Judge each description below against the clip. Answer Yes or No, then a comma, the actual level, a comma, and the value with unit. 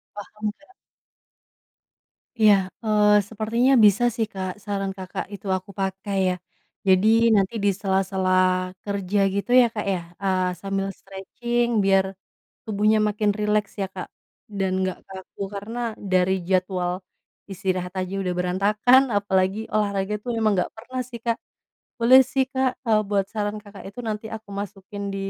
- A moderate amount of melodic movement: No, narrow, 2.1 semitones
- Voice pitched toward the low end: No, high, 200 Hz